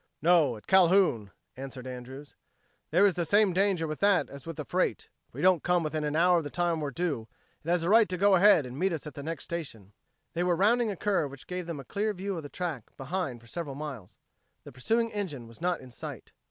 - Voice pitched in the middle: Yes, medium, 165 Hz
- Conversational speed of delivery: No, fast, 245 wpm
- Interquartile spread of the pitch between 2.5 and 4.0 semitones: No, average, 4.9 semitones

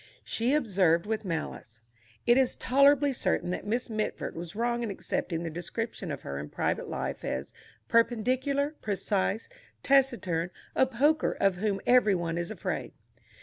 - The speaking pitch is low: No, high, 215 Hz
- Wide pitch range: Yes, wide, 6.5 semitones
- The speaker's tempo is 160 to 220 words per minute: No, average, 150 wpm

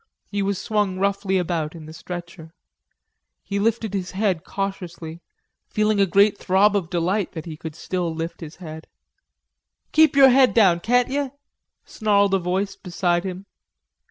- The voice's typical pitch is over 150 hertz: Yes, high, 190 Hz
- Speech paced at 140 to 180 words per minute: Yes, average, 155 wpm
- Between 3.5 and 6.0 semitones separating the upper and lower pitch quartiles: No, average, 3.1 semitones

